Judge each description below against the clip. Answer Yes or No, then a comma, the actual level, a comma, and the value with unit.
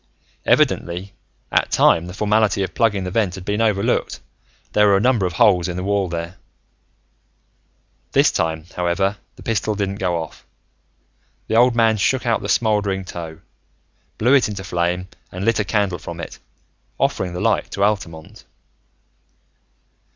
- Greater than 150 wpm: Yes, average, 160 wpm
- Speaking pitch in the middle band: No, very low, 95 Hz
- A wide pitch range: No, average, 3.2 semitones